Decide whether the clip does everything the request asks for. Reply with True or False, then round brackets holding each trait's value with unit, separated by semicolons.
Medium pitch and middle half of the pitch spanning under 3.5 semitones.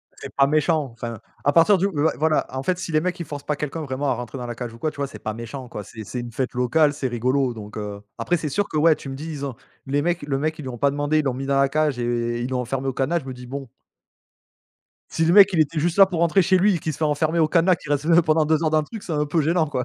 False (145 Hz; 3.8 semitones)